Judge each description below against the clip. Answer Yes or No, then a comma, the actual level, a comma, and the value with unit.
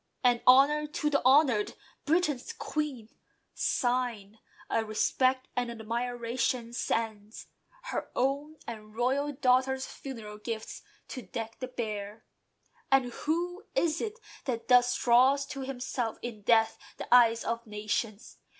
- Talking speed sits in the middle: No, slow, 125 wpm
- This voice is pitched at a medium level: No, high, 245 Hz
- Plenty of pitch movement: No, average, 3.2 semitones